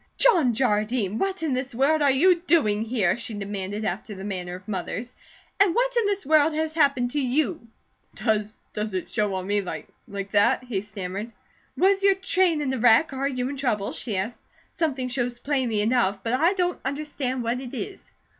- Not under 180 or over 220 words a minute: Yes, average, 190 wpm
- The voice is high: Yes, very high, 250 Hz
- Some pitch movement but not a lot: No, wide, 6.4 semitones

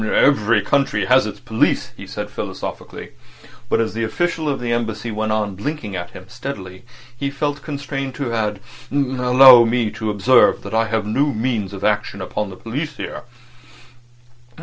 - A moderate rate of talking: Yes, average, 170 wpm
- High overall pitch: No, low, 115 Hz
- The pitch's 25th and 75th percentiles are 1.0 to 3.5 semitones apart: No, average, 4.5 semitones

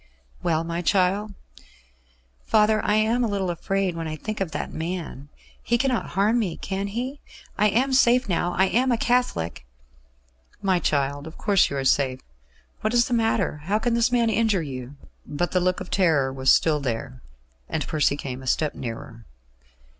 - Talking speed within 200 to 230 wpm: No, average, 185 wpm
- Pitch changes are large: Yes, wide, 7.3 semitones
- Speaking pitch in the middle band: Yes, medium, 180 Hz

